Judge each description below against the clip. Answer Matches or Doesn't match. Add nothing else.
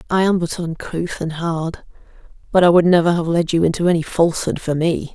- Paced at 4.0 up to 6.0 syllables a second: Matches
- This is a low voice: Doesn't match